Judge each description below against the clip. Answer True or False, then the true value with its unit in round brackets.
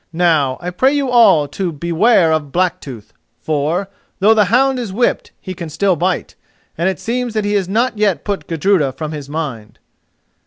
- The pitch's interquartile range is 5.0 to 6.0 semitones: True (5.5 semitones)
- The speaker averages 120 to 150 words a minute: False (185 wpm)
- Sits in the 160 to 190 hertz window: True (185 Hz)